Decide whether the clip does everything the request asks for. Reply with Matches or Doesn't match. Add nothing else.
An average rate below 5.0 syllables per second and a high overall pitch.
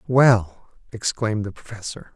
Doesn't match